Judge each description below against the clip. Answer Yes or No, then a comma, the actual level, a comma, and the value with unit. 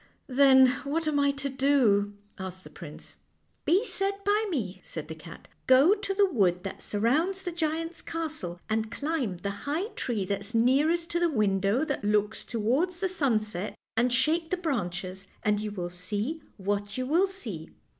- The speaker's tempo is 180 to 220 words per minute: Yes, average, 185 wpm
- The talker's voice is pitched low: No, very high, 255 Hz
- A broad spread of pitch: Yes, wide, 8.2 semitones